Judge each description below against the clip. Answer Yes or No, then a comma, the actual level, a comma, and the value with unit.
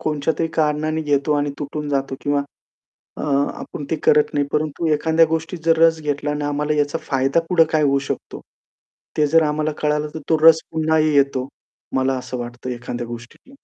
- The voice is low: No, medium, 150 Hz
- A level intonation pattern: Yes, narrow, 2.1 semitones